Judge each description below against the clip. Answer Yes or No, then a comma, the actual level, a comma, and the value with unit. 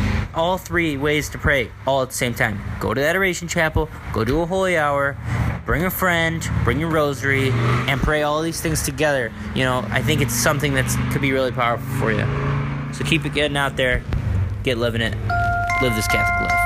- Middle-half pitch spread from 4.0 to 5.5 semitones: Yes, average, 4.3 semitones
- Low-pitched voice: Yes, low, 130 Hz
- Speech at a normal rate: No, fast, 210 wpm